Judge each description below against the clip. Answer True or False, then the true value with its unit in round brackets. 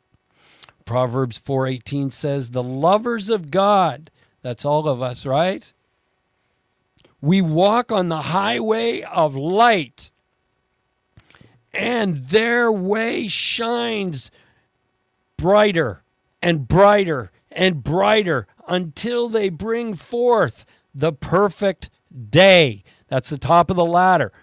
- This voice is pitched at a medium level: True (165 Hz)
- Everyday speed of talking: False (100 wpm)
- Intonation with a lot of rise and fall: True (7.9 semitones)